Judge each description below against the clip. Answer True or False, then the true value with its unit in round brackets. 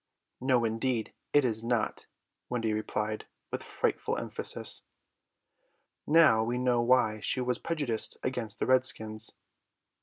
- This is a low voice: True (120 Hz)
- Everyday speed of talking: False (120 wpm)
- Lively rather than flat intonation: False (2.6 semitones)